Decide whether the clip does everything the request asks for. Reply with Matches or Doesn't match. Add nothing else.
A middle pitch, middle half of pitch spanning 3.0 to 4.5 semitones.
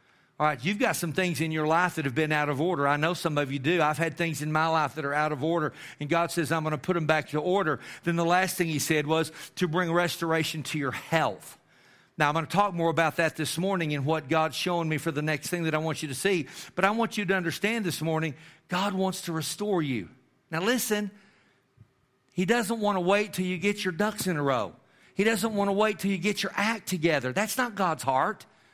Matches